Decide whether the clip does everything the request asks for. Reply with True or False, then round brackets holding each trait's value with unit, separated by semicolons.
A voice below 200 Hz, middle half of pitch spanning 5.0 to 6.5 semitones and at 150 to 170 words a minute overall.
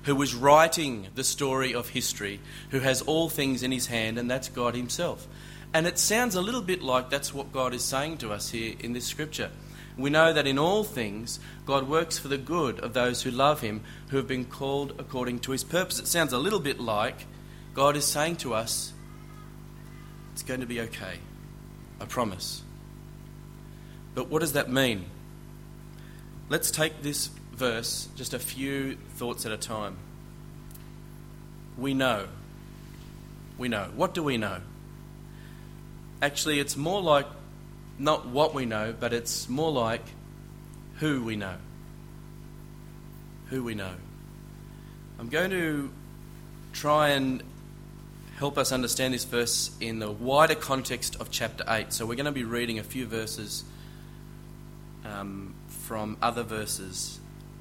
False (135 Hz; 3.7 semitones; 155 wpm)